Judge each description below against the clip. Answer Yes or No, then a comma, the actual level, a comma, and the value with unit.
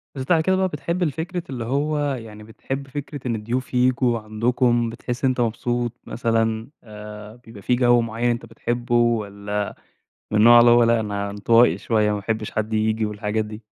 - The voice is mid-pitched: No, low, 115 Hz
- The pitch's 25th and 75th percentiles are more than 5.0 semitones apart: No, narrow, 2.5 semitones